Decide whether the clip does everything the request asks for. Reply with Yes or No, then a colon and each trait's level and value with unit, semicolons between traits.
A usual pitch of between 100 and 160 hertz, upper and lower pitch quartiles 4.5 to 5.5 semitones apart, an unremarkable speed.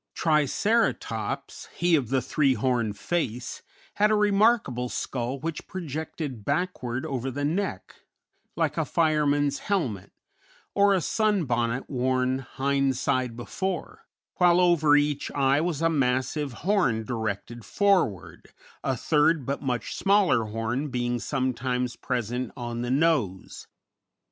No: low, 135 Hz; average, 5.2 semitones; slow, 125 wpm